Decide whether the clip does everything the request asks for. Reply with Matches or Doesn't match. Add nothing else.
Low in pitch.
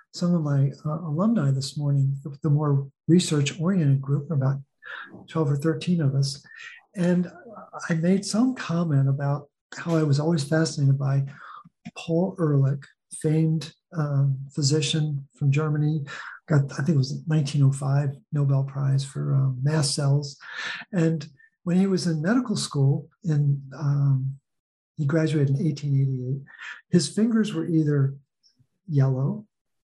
Doesn't match